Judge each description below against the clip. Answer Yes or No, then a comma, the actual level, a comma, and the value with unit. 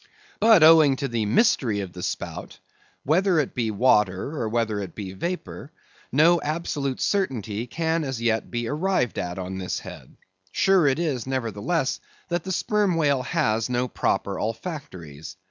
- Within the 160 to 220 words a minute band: No, average, 150 wpm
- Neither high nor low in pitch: No, low, 130 Hz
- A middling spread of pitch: No, wide, 7.0 semitones